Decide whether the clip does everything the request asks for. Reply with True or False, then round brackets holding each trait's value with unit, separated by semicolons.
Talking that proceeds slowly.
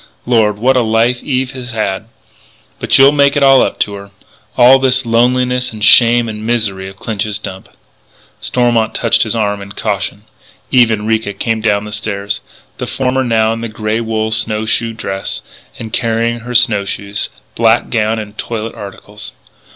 False (180 wpm)